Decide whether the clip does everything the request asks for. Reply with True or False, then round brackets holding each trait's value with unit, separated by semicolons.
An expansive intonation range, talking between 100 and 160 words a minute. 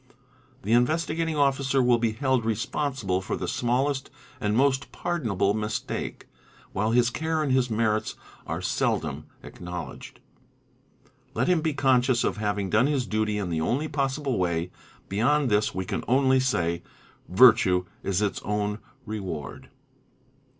False (4.7 semitones; 150 wpm)